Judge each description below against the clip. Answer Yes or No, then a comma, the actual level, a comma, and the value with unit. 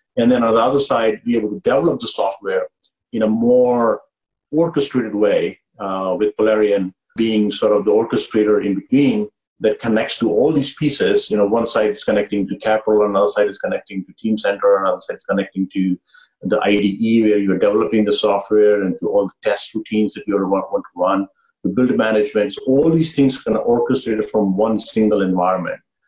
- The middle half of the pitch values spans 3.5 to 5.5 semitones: Yes, average, 3.8 semitones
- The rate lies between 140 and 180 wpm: No, fast, 205 wpm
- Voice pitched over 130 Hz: No, low, 110 Hz